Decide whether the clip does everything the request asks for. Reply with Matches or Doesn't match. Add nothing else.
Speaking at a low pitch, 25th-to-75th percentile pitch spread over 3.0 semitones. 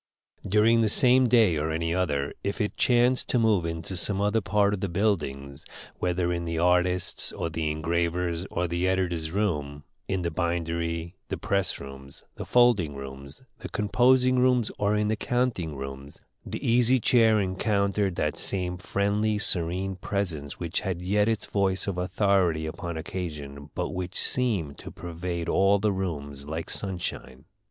Matches